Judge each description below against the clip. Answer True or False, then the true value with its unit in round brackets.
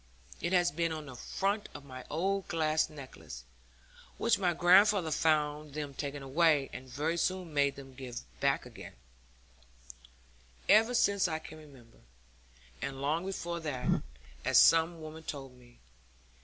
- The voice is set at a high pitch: False (155 Hz)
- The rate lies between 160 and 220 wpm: False (145 wpm)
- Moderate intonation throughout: True (3.7 semitones)